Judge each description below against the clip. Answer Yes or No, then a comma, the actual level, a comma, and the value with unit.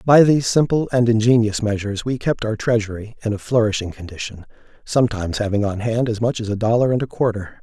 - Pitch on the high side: No, low, 115 Hz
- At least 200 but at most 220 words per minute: Yes, fast, 205 wpm